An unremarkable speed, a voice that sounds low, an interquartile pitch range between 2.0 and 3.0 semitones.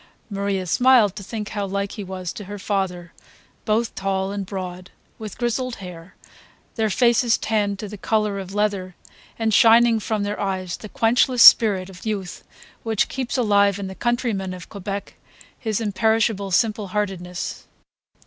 No: average, 160 wpm; high, 205 Hz; narrow, 2.6 semitones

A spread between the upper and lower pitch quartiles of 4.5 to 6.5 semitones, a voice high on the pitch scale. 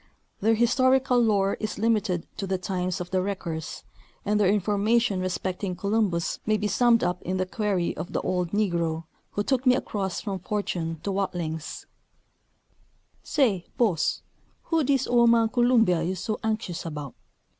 No: average, 3.9 semitones; high, 200 Hz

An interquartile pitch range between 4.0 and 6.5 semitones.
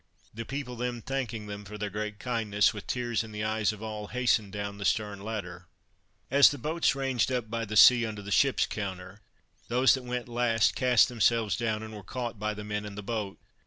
No: average, 2.8 semitones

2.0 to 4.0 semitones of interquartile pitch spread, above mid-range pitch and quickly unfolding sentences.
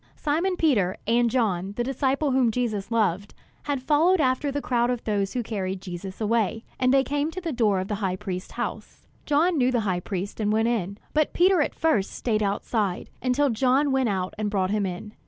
No: wide, 5.4 semitones; high, 230 Hz; fast, 210 wpm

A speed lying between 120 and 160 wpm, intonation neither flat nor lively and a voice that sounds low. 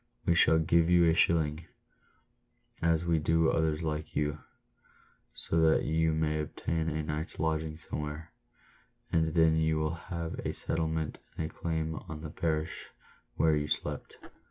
No: average, 155 wpm; narrow, 1.0 semitones; very low, 80 Hz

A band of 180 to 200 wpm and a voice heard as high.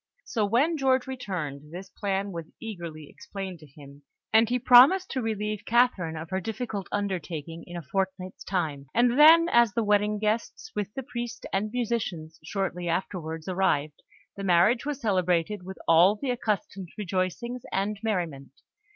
No: average, 160 wpm; high, 195 Hz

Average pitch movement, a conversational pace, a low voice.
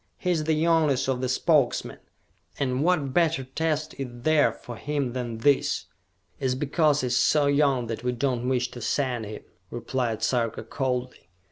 Yes: average, 3.2 semitones; average, 180 wpm; low, 130 Hz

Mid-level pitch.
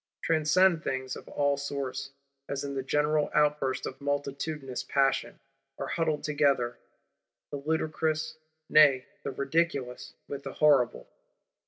Yes: medium, 145 Hz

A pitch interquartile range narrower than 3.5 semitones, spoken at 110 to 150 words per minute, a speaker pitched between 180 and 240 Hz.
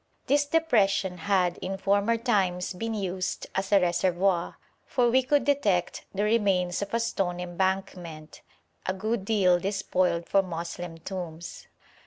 Yes: average, 3.0 semitones; average, 140 wpm; high, 190 Hz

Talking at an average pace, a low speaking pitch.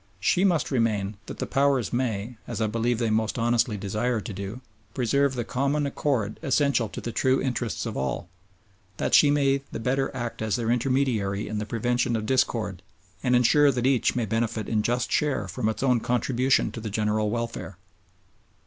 Yes: average, 185 wpm; low, 120 Hz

